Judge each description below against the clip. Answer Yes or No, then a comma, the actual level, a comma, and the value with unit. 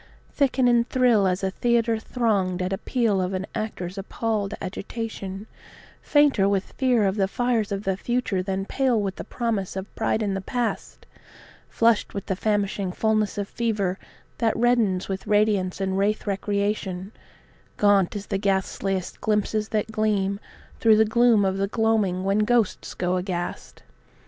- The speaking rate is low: No, average, 165 wpm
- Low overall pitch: No, high, 205 Hz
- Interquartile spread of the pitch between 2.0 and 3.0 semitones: Yes, narrow, 2.6 semitones